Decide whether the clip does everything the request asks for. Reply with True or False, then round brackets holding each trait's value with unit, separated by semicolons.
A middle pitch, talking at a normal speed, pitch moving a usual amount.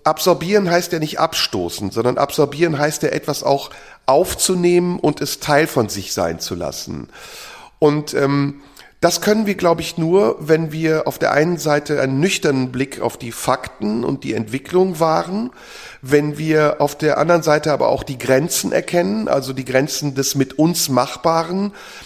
True (150 Hz; 170 wpm; 3.7 semitones)